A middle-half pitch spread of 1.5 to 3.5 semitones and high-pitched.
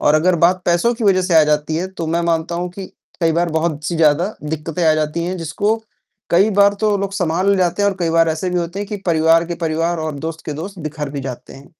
No: average, 2.7 semitones; medium, 170 Hz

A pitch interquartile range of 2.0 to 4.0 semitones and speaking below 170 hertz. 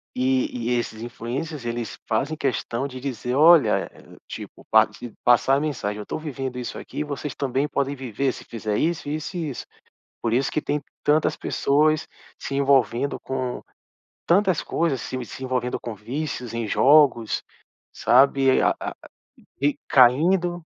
Yes: average, 3.5 semitones; low, 135 Hz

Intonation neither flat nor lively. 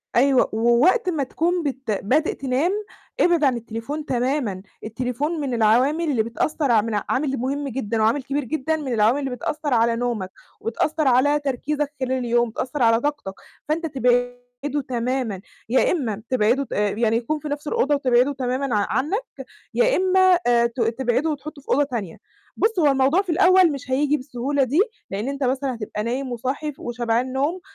Yes: average, 3.7 semitones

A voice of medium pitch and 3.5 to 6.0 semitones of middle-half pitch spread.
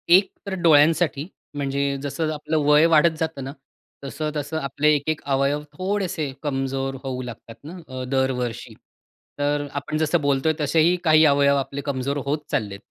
No: medium, 145 Hz; narrow, 2.6 semitones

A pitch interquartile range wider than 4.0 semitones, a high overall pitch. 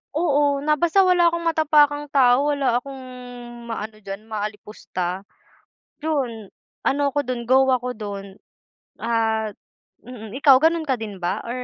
Yes: average, 5.1 semitones; very high, 255 Hz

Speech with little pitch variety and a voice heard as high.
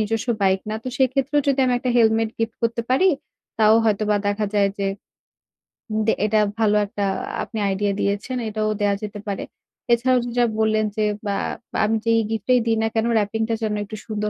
Yes: narrow, 1.9 semitones; high, 220 Hz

